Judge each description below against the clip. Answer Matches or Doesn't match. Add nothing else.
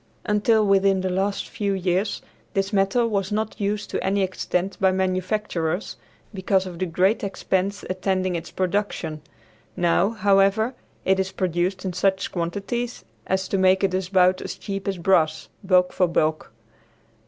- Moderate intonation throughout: Doesn't match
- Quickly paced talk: Doesn't match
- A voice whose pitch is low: Doesn't match